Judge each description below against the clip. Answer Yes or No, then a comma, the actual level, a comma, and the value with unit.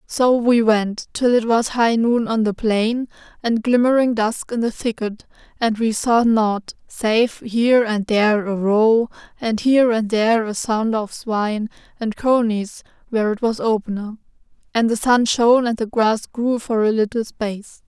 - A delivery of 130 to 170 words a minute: No, average, 180 wpm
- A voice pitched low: No, high, 225 Hz